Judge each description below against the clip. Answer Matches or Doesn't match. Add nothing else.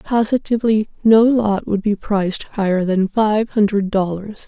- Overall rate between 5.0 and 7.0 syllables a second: Doesn't match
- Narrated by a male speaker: Doesn't match